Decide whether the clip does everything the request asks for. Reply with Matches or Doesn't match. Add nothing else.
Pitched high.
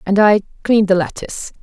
Matches